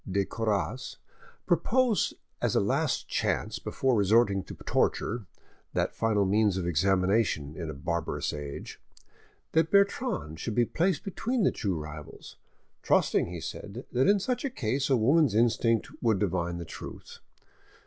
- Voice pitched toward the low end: Yes, low, 110 Hz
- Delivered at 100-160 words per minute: Yes, average, 150 wpm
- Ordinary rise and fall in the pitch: No, wide, 7.0 semitones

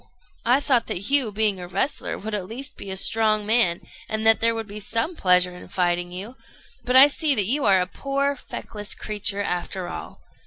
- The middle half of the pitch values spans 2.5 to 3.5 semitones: No, average, 4.8 semitones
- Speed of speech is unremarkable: No, fast, 210 wpm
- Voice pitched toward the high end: Yes, high, 215 Hz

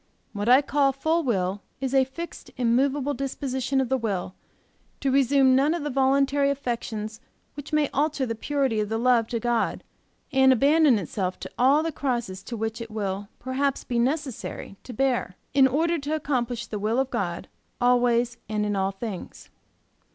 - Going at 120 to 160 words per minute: No, average, 175 wpm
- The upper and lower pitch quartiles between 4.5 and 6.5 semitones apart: No, average, 3.8 semitones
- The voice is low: No, very high, 255 Hz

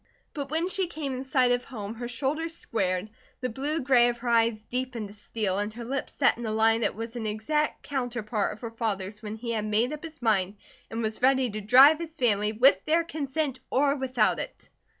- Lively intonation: No, average, 4.1 semitones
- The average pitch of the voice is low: No, high, 240 Hz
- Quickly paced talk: Yes, fast, 220 wpm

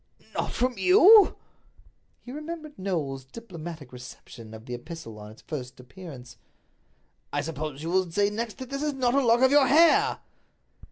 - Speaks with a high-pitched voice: No, medium, 180 Hz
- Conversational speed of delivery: Yes, average, 170 wpm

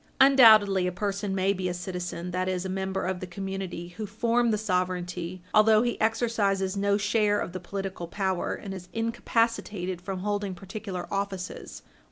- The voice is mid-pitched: No, high, 195 Hz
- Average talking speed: Yes, average, 170 wpm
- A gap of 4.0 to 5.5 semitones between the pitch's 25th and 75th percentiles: No, narrow, 2.4 semitones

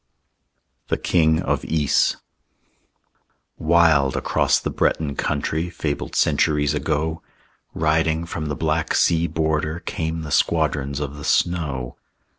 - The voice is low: Yes, very low, 80 Hz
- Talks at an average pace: No, slow, 115 wpm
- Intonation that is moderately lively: No, narrow, 1.8 semitones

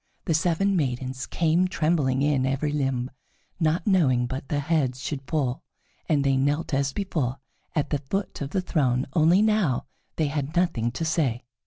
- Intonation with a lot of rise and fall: No, average, 3.8 semitones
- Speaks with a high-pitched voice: No, medium, 145 Hz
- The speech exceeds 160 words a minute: Yes, average, 170 wpm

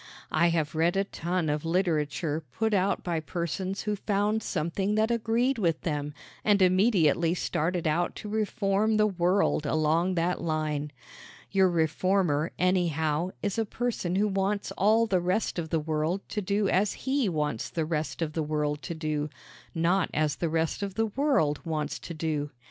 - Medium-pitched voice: Yes, medium, 175 Hz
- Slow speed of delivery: No, average, 170 wpm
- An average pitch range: Yes, average, 4.2 semitones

